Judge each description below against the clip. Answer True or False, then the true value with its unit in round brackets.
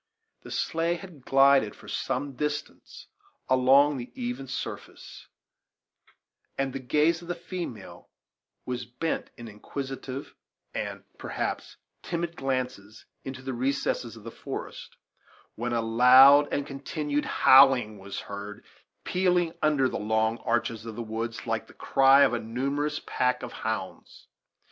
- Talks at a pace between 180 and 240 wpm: False (135 wpm)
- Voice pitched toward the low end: True (130 Hz)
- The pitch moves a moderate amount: True (3.8 semitones)